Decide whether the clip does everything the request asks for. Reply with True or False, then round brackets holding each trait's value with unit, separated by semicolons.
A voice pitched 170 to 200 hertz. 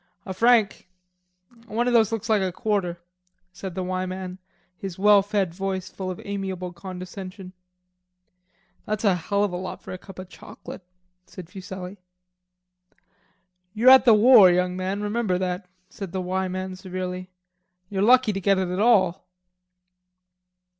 True (190 Hz)